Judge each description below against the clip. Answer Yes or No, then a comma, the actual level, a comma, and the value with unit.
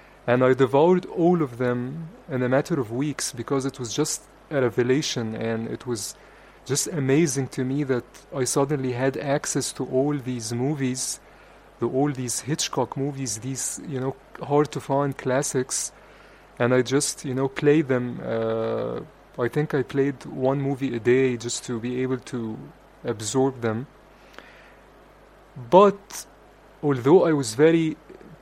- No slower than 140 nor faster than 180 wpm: Yes, average, 150 wpm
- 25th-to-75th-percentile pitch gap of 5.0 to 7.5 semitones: No, narrow, 2.6 semitones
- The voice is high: No, low, 135 Hz